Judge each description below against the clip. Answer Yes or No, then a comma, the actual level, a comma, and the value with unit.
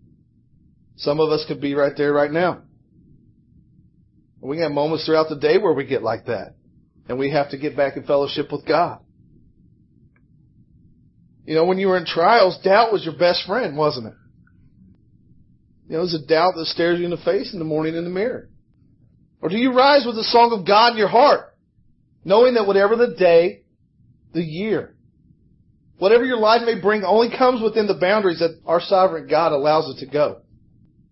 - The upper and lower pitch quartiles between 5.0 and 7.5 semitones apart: Yes, wide, 5.4 semitones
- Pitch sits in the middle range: Yes, medium, 165 Hz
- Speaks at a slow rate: No, average, 190 wpm